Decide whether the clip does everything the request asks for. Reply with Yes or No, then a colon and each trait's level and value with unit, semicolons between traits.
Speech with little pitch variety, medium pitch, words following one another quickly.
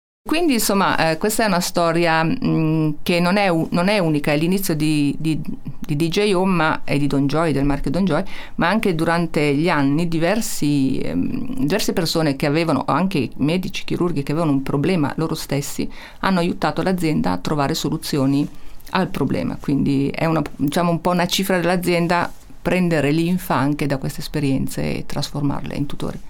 No: average, 3.7 semitones; medium, 165 Hz; fast, 180 wpm